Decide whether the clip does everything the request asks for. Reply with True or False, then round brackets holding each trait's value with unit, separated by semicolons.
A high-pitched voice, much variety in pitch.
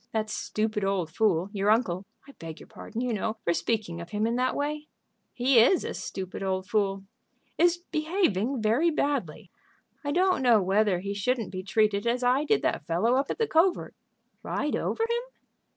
True (220 Hz; 6.4 semitones)